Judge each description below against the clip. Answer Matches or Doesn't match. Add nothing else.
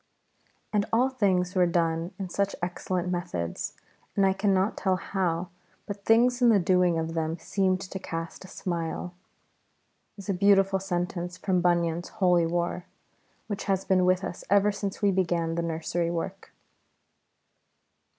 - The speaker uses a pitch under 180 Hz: Doesn't match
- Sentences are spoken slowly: Doesn't match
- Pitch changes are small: Matches